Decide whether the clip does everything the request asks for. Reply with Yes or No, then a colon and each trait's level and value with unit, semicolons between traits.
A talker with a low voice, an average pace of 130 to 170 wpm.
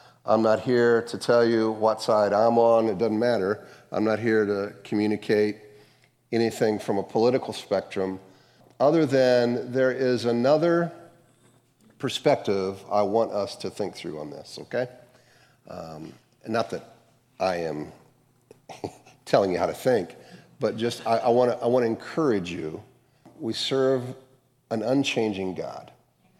Yes: low, 115 Hz; average, 145 wpm